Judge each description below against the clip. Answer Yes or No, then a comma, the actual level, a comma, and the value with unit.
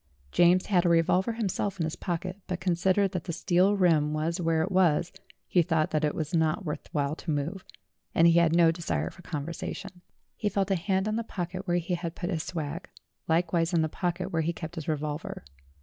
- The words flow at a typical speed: No, fast, 220 wpm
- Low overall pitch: No, medium, 170 Hz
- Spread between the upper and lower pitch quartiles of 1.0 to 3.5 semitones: Yes, narrow, 2.4 semitones